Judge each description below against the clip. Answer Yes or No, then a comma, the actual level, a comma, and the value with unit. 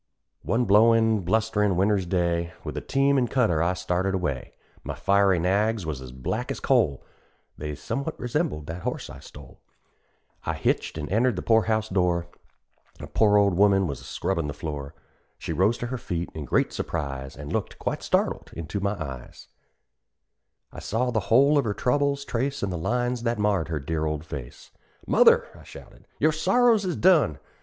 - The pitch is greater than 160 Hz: No, low, 100 Hz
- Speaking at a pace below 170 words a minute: No, average, 180 wpm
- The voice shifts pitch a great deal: Yes, wide, 6.6 semitones